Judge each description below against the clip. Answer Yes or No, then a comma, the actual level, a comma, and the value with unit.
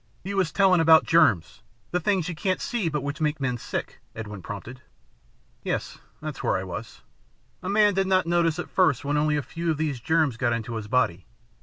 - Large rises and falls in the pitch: Yes, wide, 6.5 semitones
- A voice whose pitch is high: No, medium, 155 Hz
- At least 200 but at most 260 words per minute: Yes, fast, 205 wpm